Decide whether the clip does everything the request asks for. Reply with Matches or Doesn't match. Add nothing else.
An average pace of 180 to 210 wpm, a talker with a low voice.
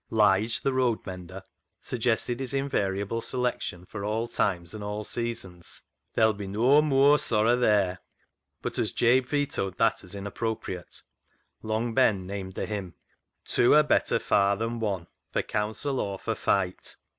Doesn't match